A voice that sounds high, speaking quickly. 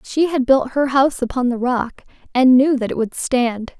Yes: very high, 260 Hz; fast, 220 wpm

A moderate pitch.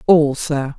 Yes: medium, 150 Hz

